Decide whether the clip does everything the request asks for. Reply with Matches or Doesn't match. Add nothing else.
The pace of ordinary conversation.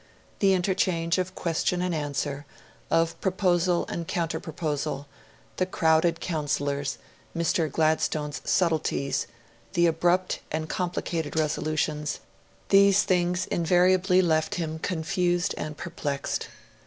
Doesn't match